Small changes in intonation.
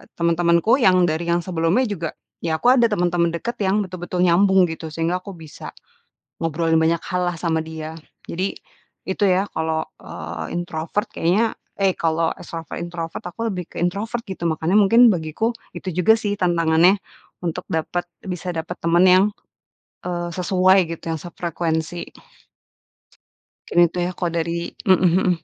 Yes: narrow, 2.3 semitones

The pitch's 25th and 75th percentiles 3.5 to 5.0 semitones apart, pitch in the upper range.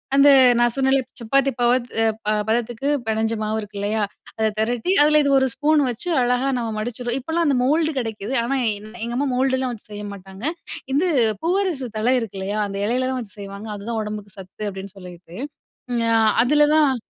Yes: average, 4.3 semitones; high, 240 Hz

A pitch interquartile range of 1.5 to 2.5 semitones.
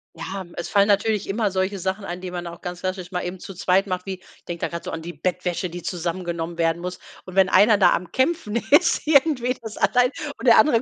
No: average, 2.9 semitones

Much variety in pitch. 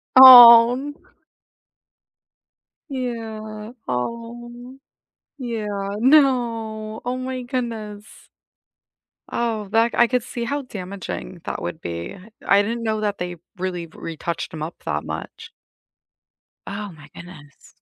No: average, 3.7 semitones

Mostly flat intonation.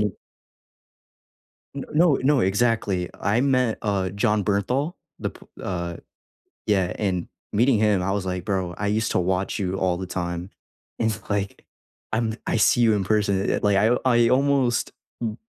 No: average, 3.7 semitones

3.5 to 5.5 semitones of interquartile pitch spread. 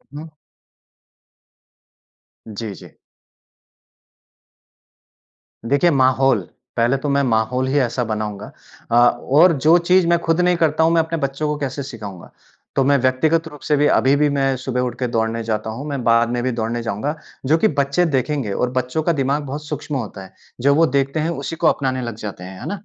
Yes: average, 4.2 semitones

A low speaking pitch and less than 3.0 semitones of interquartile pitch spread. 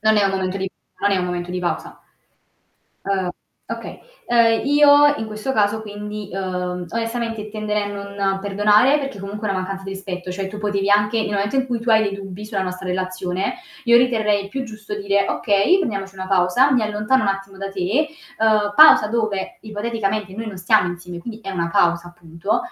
No: high, 205 Hz; narrow, 2.5 semitones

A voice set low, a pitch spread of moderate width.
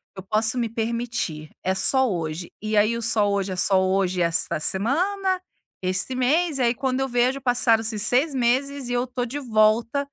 No: high, 235 Hz; average, 4.8 semitones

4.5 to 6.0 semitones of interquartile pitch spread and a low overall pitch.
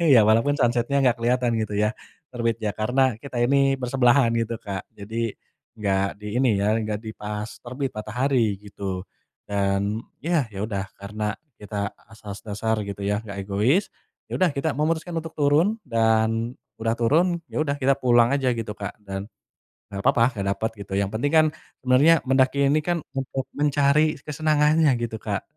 Yes: average, 4.8 semitones; low, 115 Hz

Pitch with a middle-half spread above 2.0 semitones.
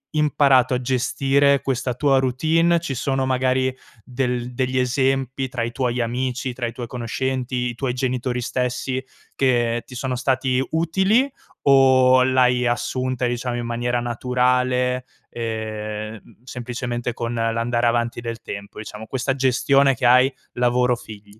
No: narrow, 1.6 semitones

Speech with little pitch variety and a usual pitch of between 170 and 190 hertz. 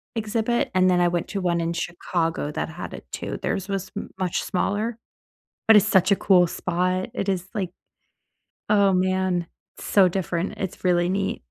Yes: narrow, 2.1 semitones; medium, 185 Hz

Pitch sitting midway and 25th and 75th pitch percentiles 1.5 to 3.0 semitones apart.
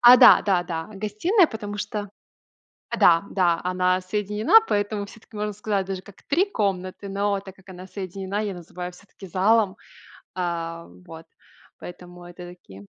No: high, 195 Hz; narrow, 2.6 semitones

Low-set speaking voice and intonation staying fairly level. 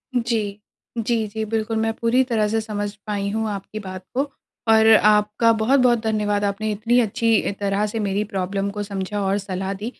No: high, 210 Hz; narrow, 1.9 semitones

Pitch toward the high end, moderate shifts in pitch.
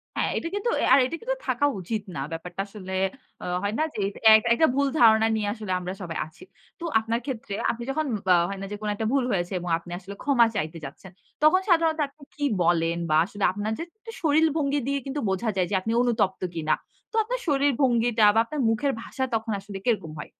No: high, 225 Hz; wide, 6.7 semitones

